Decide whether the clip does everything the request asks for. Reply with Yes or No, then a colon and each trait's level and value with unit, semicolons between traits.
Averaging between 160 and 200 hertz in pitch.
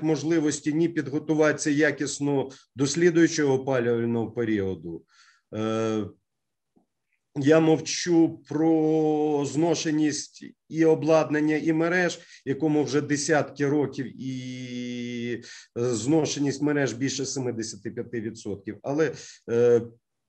No: medium, 145 Hz